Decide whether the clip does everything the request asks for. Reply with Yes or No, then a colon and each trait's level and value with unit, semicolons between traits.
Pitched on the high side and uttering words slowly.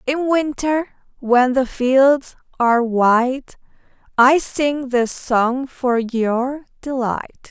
Yes: very high, 260 Hz; slow, 110 wpm